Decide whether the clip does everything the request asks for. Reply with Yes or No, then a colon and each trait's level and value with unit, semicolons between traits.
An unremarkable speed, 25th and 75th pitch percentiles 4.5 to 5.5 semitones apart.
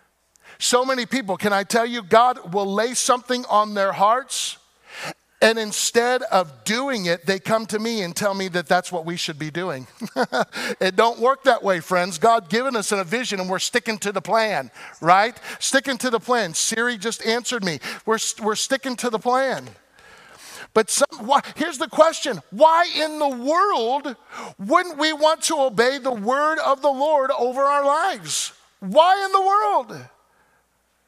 Yes: average, 180 wpm; average, 4.9 semitones